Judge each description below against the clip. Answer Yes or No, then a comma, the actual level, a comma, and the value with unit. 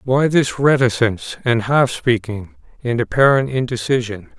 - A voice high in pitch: No, low, 125 Hz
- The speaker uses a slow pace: Yes, slow, 125 wpm